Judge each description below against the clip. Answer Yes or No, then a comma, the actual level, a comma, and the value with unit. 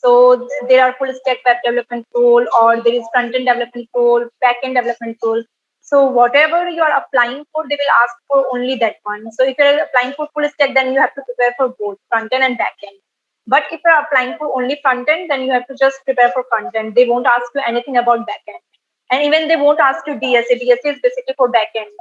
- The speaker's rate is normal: No, fast, 250 wpm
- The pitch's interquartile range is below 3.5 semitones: Yes, average, 2.9 semitones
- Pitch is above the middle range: Yes, very high, 255 Hz